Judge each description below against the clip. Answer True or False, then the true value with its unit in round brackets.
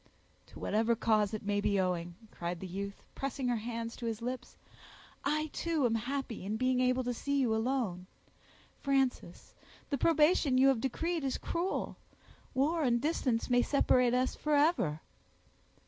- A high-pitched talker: True (250 Hz)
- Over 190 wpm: False (160 wpm)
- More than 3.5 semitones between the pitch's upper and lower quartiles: True (4.0 semitones)